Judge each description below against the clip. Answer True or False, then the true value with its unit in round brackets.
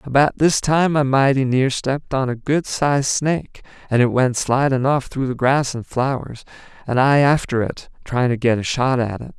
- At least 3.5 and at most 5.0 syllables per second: True (4.9 syllables/s)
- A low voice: True (130 Hz)